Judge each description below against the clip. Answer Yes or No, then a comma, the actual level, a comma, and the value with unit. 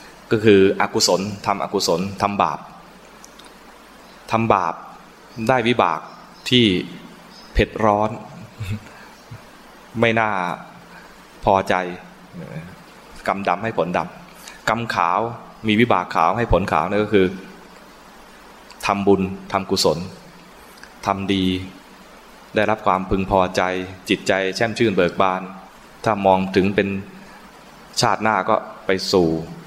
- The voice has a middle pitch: No, low, 100 Hz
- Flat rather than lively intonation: Yes, narrow, 2.0 semitones